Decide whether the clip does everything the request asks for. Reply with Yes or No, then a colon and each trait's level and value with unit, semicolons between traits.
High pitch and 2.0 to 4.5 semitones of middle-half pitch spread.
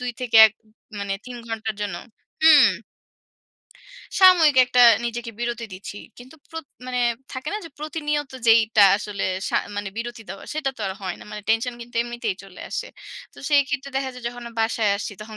Yes: high, 240 Hz; average, 4.2 semitones